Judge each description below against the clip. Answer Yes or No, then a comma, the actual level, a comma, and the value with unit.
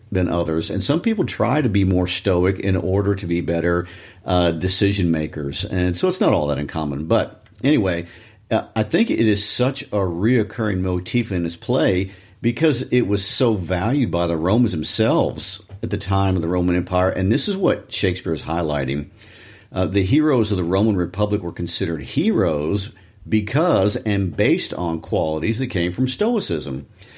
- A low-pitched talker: Yes, very low, 95 Hz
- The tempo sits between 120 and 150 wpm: No, average, 175 wpm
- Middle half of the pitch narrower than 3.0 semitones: No, average, 4.0 semitones